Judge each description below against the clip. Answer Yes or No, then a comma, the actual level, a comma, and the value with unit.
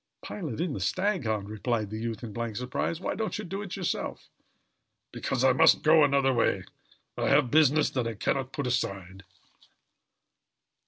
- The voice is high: No, low, 130 Hz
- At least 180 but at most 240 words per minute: No, average, 170 wpm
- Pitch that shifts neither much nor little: No, wide, 6.0 semitones